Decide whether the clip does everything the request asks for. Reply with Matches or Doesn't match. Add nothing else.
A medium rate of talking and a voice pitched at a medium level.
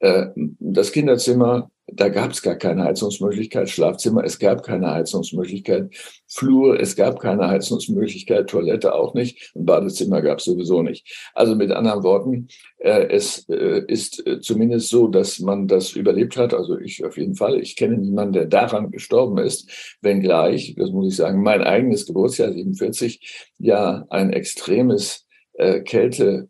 Doesn't match